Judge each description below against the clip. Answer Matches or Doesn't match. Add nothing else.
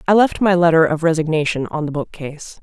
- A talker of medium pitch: Matches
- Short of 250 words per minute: Matches